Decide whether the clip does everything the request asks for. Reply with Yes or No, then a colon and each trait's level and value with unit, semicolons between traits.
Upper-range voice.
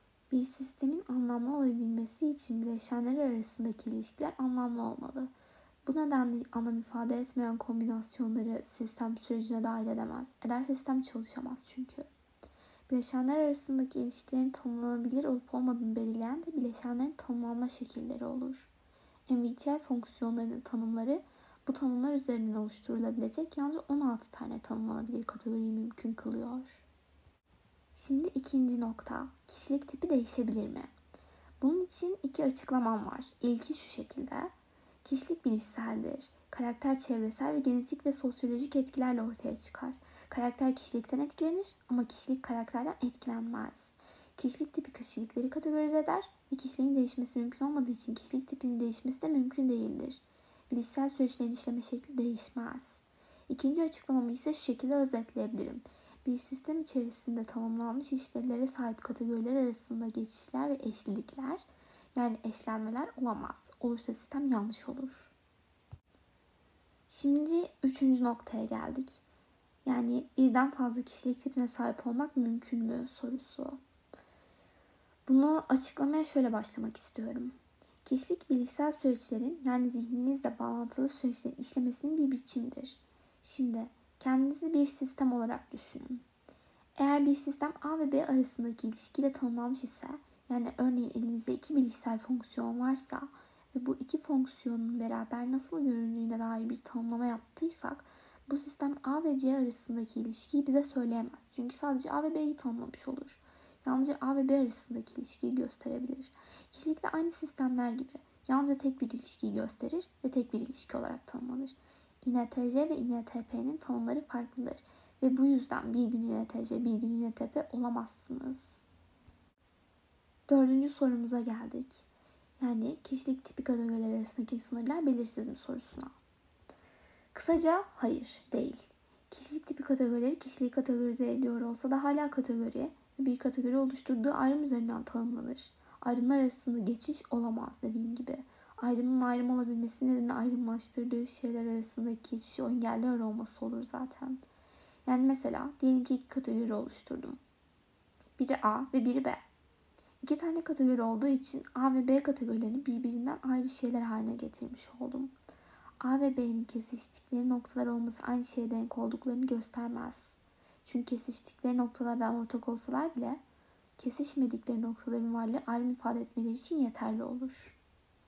Yes: very high, 255 Hz